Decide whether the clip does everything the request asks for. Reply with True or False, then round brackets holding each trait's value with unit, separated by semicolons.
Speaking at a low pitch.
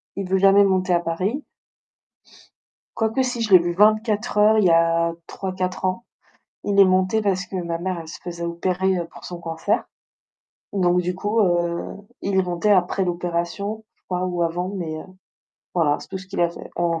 False (185 Hz)